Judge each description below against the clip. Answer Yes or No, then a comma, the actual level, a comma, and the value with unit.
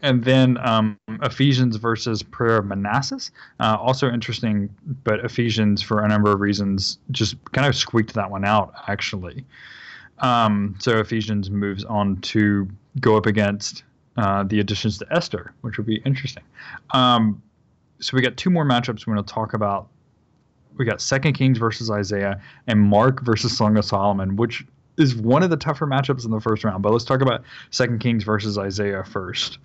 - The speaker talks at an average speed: Yes, average, 180 wpm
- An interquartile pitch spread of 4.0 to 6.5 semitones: No, average, 3.5 semitones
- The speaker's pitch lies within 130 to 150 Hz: No, low, 110 Hz